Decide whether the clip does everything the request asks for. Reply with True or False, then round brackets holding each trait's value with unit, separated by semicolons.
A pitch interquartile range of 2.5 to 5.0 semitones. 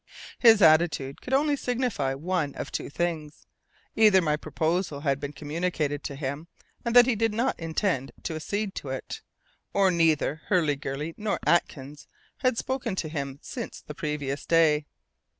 False (5.5 semitones)